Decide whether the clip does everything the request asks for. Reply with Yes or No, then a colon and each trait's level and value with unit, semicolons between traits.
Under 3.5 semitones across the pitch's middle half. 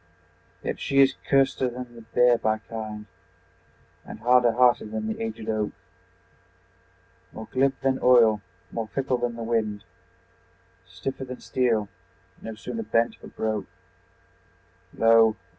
Yes: narrow, 2.5 semitones